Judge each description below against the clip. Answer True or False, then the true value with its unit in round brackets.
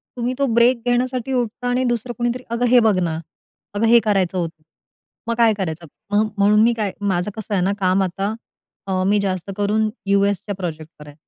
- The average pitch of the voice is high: True (205 Hz)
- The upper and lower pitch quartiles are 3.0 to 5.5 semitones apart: True (4.0 semitones)